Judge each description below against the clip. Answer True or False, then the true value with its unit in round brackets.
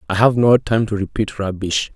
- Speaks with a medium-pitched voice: False (105 Hz)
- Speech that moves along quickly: True (215 wpm)